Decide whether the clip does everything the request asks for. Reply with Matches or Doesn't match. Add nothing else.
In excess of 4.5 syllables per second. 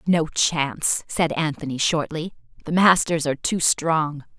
Doesn't match